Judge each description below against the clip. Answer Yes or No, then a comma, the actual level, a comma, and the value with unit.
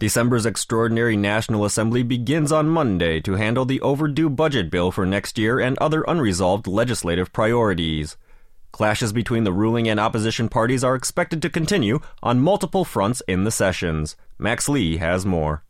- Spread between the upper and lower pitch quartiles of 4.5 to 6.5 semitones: Yes, average, 5.1 semitones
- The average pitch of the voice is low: Yes, low, 115 Hz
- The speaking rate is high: No, average, 160 wpm